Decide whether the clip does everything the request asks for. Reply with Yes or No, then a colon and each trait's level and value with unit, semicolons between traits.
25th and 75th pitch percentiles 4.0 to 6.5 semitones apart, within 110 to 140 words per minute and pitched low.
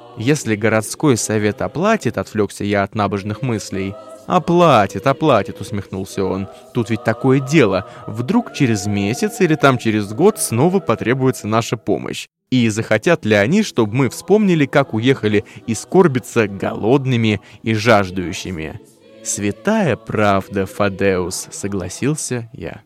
Yes: average, 5.2 semitones; average, 125 wpm; low, 115 Hz